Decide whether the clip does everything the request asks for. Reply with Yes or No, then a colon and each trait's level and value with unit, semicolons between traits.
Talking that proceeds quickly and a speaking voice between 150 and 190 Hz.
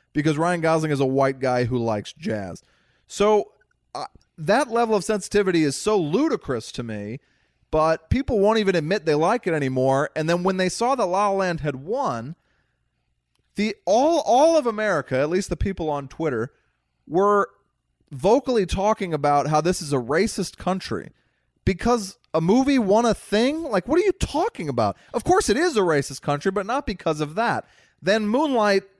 No: average, 180 wpm; medium, 185 Hz